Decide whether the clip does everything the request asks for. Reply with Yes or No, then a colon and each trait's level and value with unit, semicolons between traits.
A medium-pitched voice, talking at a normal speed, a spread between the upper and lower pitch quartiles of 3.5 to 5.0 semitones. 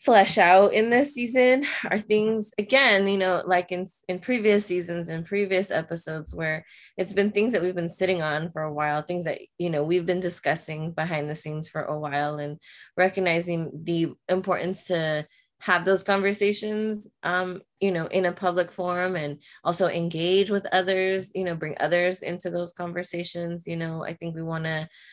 No: medium, 180 Hz; average, 185 wpm; average, 2.9 semitones